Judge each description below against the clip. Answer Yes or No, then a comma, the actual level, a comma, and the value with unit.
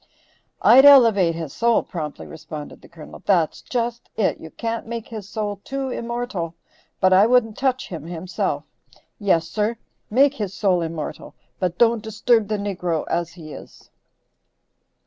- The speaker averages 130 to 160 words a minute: Yes, average, 150 wpm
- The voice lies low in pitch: No, high, 205 Hz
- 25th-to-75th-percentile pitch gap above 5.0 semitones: Yes, wide, 5.5 semitones